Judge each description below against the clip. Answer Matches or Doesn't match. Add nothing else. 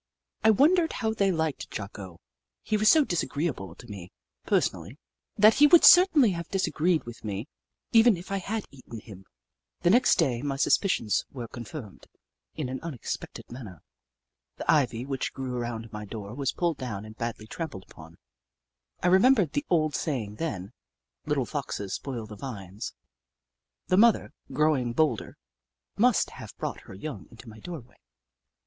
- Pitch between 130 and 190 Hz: Matches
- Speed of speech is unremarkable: Matches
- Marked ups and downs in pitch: Matches